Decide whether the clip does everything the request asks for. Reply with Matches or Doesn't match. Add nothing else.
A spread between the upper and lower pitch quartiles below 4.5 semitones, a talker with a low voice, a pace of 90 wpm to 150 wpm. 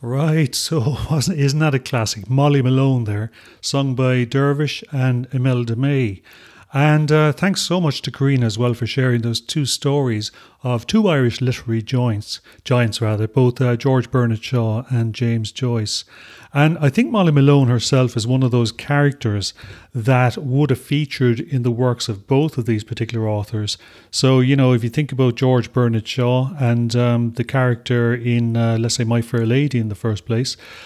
Doesn't match